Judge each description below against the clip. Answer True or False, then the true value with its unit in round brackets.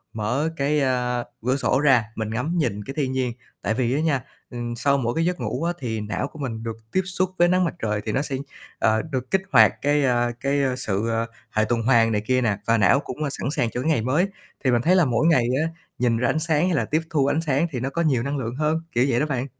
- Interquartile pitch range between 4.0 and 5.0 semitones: True (4.4 semitones)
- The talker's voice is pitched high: False (130 Hz)